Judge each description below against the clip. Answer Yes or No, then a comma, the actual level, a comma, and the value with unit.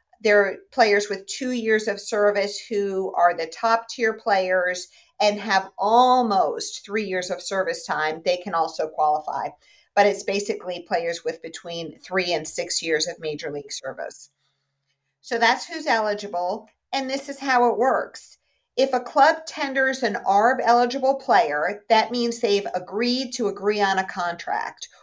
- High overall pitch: Yes, high, 205 Hz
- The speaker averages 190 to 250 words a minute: No, average, 160 wpm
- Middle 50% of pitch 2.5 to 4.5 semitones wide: No, average, 5.0 semitones